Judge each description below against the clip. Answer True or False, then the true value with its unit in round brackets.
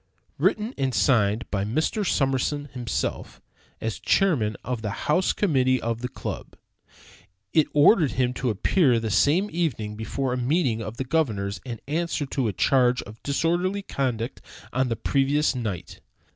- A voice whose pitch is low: True (130 Hz)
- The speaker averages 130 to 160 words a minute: True (155 wpm)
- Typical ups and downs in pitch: True (5.0 semitones)